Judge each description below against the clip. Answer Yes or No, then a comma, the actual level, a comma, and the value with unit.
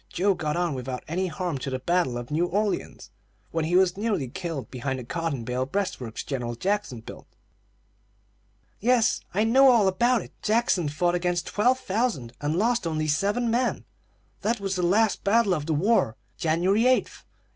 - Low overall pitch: No, medium, 180 Hz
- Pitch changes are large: Yes, wide, 6.2 semitones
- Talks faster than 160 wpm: Yes, average, 180 wpm